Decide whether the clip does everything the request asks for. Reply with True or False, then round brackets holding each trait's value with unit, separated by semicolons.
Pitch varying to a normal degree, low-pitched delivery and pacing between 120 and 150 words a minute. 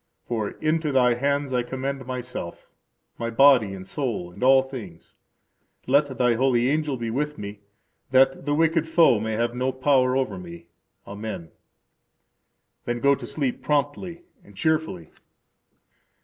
True (3.8 semitones; 130 Hz; 145 wpm)